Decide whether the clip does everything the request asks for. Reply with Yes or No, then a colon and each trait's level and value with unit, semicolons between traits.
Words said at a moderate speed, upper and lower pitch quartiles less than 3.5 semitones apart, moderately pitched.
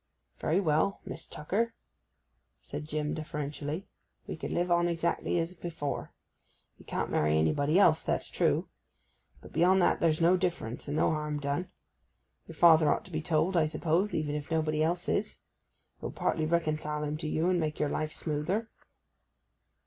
Yes: average, 170 wpm; narrow, 2.4 semitones; medium, 155 Hz